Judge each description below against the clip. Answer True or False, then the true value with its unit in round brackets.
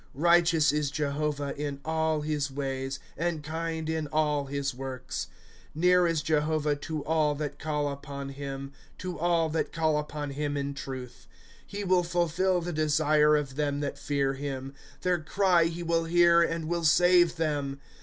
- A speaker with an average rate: True (175 wpm)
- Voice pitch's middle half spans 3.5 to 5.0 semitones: False (2.7 semitones)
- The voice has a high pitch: False (150 Hz)